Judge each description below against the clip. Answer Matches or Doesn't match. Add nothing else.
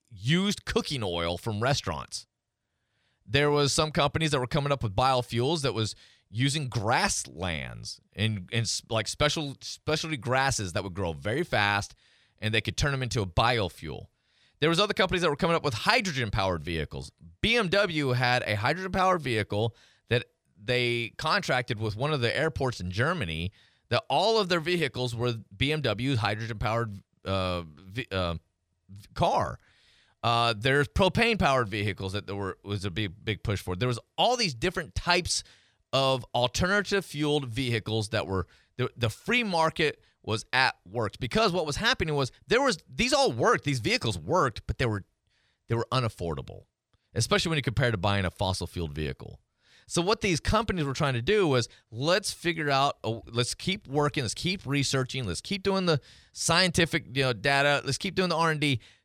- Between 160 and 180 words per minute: Matches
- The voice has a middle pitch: Doesn't match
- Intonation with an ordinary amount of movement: Doesn't match